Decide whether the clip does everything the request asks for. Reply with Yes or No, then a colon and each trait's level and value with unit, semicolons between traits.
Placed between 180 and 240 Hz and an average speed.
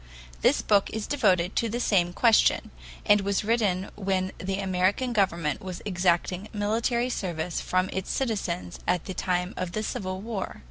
Yes: high, 190 Hz; average, 165 wpm